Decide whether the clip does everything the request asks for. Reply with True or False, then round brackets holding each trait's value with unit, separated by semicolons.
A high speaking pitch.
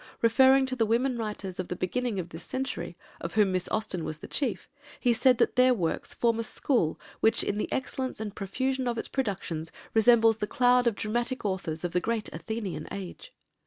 True (225 Hz)